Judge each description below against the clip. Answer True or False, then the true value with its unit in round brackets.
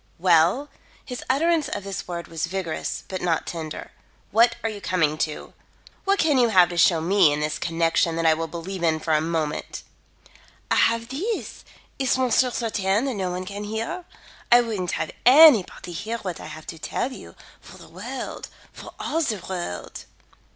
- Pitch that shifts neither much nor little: False (6.3 semitones)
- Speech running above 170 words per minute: True (185 wpm)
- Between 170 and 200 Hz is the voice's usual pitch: True (190 Hz)